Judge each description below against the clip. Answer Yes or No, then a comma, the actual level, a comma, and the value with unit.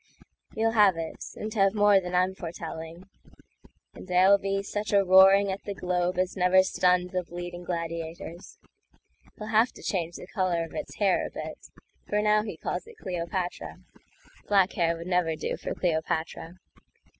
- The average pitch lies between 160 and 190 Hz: Yes, medium, 185 Hz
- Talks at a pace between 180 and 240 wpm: No, average, 150 wpm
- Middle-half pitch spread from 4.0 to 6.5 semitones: No, narrow, 2.5 semitones